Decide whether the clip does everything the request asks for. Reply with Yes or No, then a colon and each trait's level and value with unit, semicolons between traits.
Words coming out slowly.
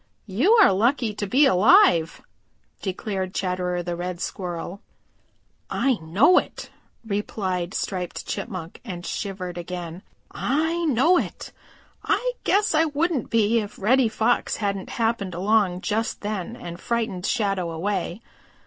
Yes: slow, 130 wpm